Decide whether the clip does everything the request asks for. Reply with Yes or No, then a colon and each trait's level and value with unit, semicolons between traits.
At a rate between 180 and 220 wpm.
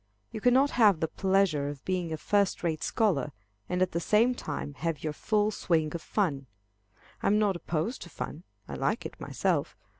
Yes: average, 190 wpm